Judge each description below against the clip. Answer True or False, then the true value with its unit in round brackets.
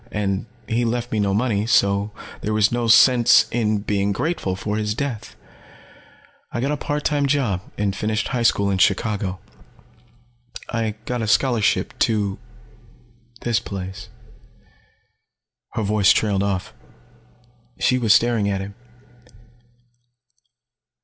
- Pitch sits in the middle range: False (105 Hz)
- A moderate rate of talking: False (125 wpm)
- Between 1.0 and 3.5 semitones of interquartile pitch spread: True (3.0 semitones)